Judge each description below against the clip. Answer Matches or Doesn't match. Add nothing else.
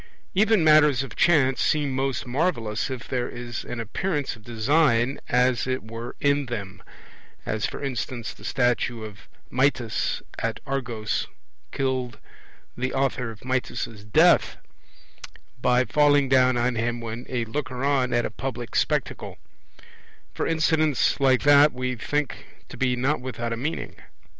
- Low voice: Matches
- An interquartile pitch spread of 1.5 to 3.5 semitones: Matches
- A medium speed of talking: Matches